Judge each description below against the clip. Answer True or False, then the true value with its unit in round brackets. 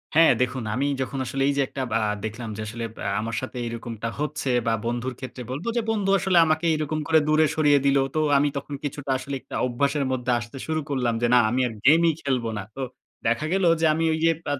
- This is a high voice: False (135 Hz)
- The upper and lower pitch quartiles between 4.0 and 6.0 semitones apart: True (4.3 semitones)